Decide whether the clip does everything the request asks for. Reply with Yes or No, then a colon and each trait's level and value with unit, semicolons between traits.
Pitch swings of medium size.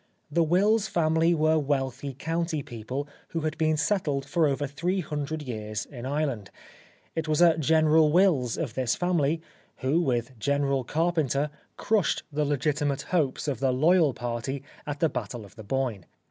Yes: average, 3.5 semitones